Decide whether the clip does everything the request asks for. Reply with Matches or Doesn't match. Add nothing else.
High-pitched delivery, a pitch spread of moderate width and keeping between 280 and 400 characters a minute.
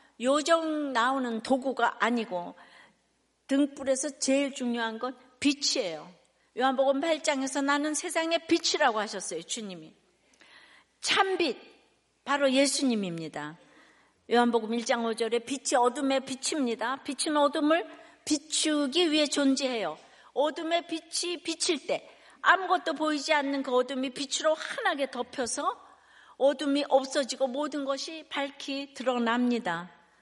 Doesn't match